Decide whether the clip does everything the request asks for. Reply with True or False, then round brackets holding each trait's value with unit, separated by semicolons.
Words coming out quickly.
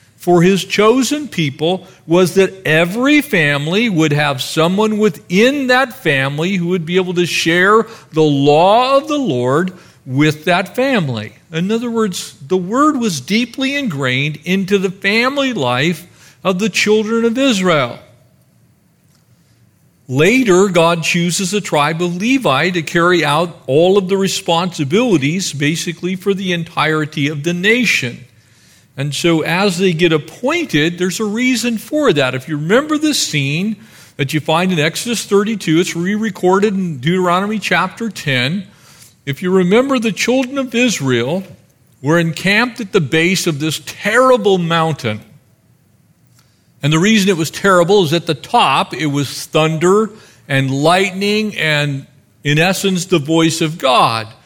False (145 wpm)